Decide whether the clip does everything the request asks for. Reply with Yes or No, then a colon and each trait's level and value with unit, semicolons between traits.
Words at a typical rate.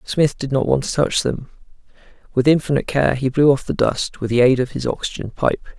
No: fast, 230 wpm